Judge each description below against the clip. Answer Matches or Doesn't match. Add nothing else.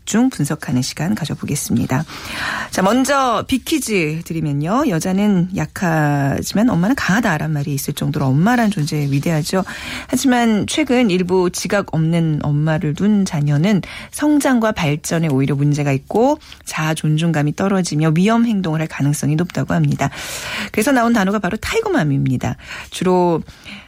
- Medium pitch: Matches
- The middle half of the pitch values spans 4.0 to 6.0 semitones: Doesn't match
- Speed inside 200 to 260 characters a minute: Doesn't match